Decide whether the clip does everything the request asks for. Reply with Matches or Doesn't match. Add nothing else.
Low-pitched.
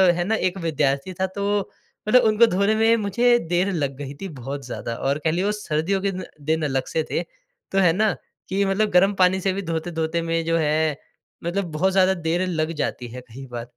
Doesn't match